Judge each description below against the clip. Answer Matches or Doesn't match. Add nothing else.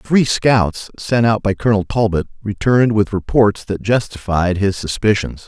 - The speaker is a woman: Doesn't match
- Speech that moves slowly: Doesn't match